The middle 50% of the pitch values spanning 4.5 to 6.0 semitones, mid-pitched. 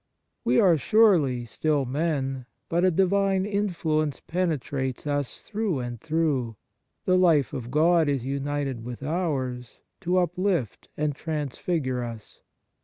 Yes: average, 5.3 semitones; medium, 150 Hz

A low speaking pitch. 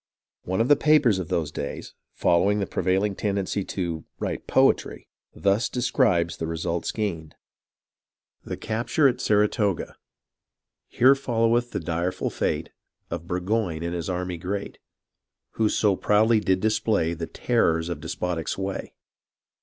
Yes: very low, 95 Hz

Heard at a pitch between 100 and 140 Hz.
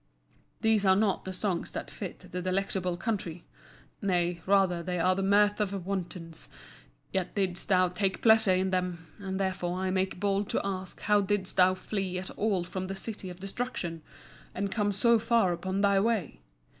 No: high, 190 Hz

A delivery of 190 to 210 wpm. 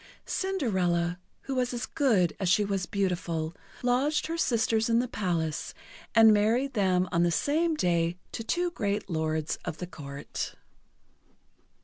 No: average, 145 wpm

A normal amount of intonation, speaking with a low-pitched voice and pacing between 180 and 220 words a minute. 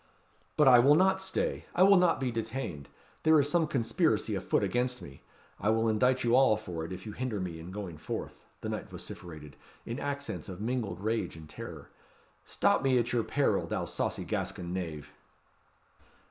No: wide, 6.5 semitones; low, 115 Hz; average, 190 wpm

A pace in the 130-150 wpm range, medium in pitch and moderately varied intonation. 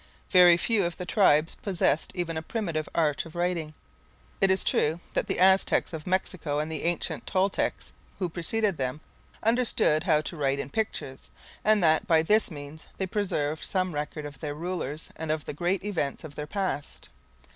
No: average, 180 wpm; medium, 165 Hz; average, 3.7 semitones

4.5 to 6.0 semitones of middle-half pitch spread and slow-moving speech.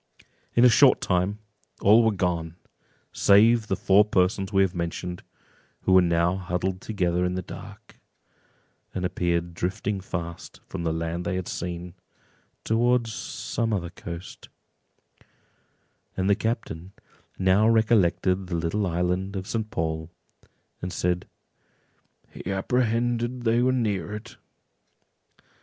No: average, 3.8 semitones; slow, 125 wpm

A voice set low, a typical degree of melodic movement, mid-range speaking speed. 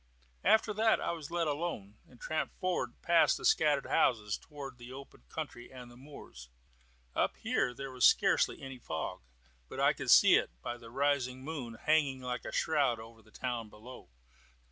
Yes: low, 130 Hz; average, 3.7 semitones; average, 180 wpm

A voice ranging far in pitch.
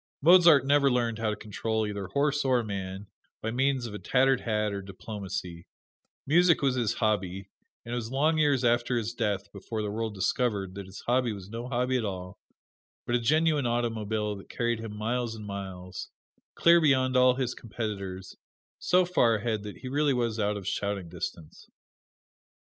No: average, 4.0 semitones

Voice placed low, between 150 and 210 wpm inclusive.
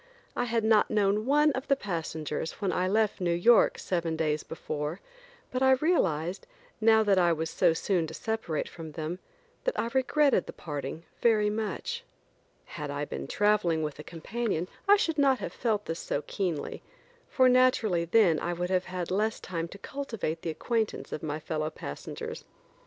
No: medium, 185 Hz; average, 180 wpm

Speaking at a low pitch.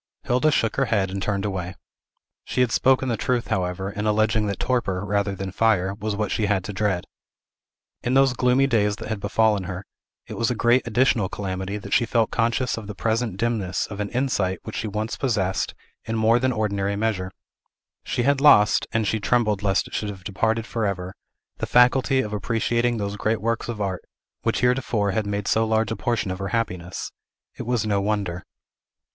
Yes: low, 105 Hz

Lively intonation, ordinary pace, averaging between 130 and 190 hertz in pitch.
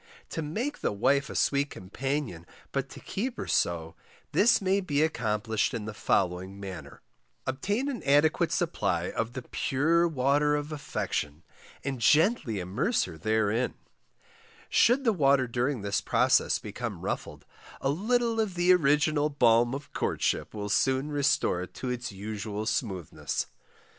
Yes: wide, 6.7 semitones; average, 150 wpm; low, 135 Hz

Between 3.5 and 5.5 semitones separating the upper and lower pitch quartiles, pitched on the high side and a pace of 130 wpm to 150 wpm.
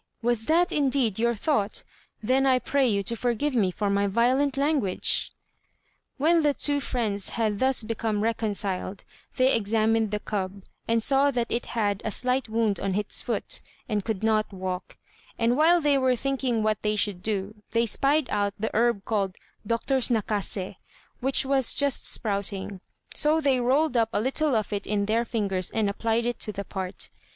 No: average, 4.3 semitones; high, 225 Hz; average, 180 wpm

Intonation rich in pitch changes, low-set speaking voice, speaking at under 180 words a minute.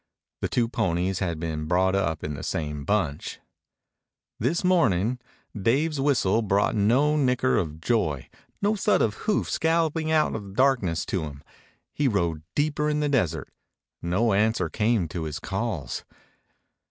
Yes: wide, 8.3 semitones; low, 105 Hz; average, 155 wpm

